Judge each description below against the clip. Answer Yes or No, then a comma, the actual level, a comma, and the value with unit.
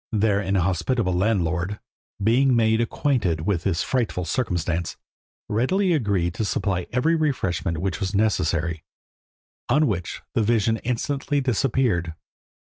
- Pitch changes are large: Yes, wide, 5.9 semitones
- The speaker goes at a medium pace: No, slow, 120 wpm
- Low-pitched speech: Yes, low, 105 Hz